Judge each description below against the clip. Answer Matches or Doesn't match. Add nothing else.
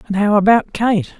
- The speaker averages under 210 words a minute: Matches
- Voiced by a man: Doesn't match